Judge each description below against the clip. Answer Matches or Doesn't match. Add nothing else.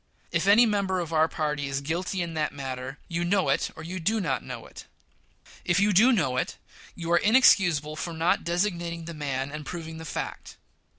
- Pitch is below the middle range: Doesn't match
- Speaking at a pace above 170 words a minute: Matches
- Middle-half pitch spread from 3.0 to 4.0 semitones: Matches